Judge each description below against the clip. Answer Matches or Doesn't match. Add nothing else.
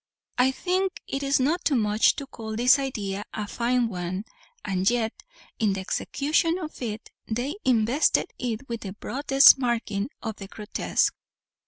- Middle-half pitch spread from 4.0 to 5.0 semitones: Matches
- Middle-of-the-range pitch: Doesn't match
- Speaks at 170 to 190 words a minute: Doesn't match